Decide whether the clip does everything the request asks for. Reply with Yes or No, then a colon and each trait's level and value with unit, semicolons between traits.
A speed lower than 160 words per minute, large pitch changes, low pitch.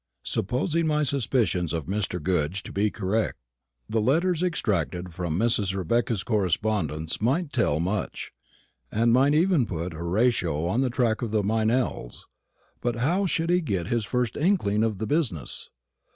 Yes: average, 150 wpm; wide, 6.2 semitones; low, 110 Hz